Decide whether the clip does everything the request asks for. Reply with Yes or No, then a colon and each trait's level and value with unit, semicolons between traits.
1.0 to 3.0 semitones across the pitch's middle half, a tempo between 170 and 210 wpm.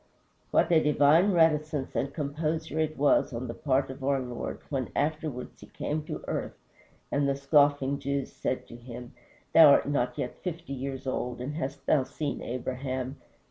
Yes: average, 2.7 semitones; average, 175 wpm